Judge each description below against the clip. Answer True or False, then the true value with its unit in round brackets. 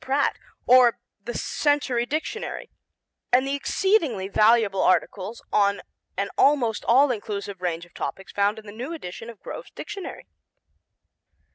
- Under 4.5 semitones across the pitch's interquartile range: False (5.5 semitones)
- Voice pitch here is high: True (235 Hz)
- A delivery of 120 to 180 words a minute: True (135 wpm)